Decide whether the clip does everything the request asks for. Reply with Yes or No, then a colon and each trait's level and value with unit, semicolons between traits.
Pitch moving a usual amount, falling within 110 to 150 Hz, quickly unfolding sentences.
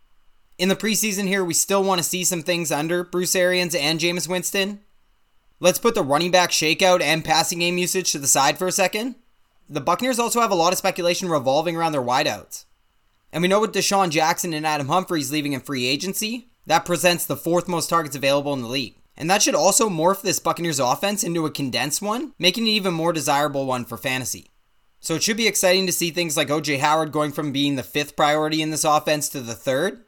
No: average, 3.8 semitones; medium, 170 Hz; fast, 220 wpm